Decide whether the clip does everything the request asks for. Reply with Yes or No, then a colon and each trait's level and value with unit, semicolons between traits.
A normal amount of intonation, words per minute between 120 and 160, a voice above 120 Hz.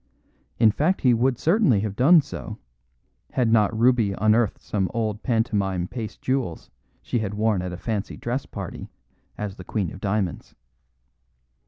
No: average, 3.7 semitones; average, 155 wpm; low, 110 Hz